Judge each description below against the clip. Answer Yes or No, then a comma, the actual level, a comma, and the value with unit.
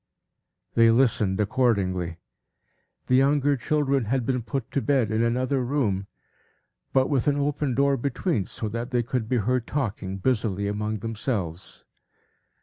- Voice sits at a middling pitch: No, low, 120 Hz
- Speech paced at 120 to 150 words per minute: Yes, average, 145 wpm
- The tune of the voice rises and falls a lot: No, average, 4.1 semitones